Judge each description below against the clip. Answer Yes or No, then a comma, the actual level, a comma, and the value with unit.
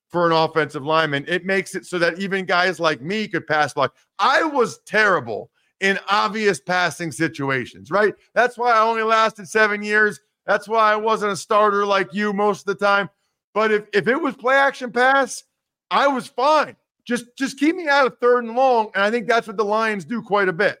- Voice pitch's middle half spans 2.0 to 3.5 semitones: No, average, 4.3 semitones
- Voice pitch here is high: Yes, high, 210 Hz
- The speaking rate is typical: No, fast, 215 wpm